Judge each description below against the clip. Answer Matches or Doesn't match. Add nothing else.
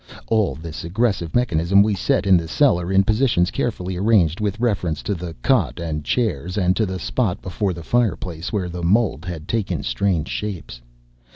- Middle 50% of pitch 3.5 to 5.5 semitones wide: Matches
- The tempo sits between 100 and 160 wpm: Doesn't match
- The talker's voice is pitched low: Matches